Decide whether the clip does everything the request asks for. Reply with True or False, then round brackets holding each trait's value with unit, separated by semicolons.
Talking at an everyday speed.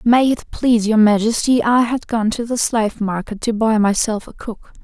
False (210 wpm)